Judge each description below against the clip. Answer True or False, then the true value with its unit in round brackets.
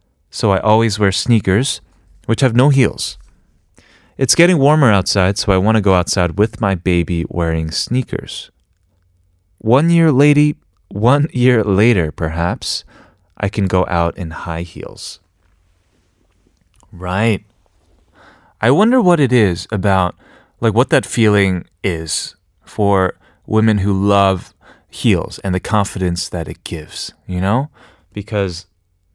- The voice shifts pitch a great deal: False (4.4 semitones)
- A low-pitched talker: True (95 Hz)